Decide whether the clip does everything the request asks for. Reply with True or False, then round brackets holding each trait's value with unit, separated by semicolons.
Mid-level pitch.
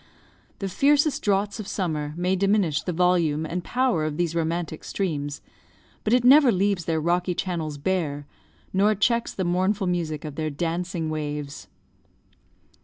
True (175 Hz)